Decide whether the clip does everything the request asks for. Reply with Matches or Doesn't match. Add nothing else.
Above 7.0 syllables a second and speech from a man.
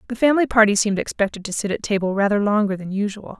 Doesn't match